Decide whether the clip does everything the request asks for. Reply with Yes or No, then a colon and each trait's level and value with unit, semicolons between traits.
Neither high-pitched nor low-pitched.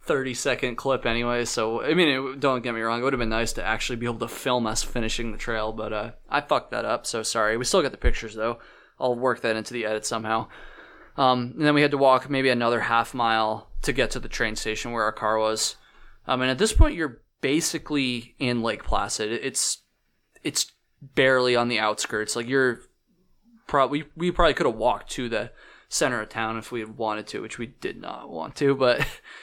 No: low, 120 Hz